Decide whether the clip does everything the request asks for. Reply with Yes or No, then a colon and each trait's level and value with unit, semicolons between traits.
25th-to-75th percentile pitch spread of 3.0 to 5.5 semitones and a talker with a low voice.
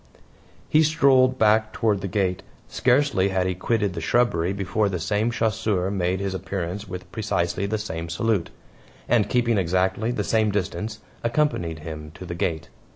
Yes: average, 3.7 semitones; low, 100 Hz